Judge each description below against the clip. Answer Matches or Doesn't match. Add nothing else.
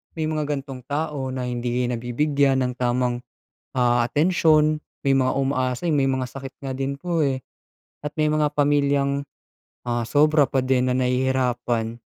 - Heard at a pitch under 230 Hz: Matches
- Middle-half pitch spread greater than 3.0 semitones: Doesn't match